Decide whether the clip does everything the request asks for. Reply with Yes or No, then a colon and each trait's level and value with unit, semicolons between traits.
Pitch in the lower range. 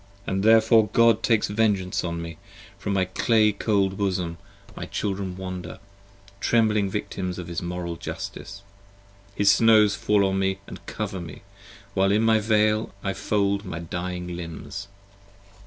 Yes: low, 100 Hz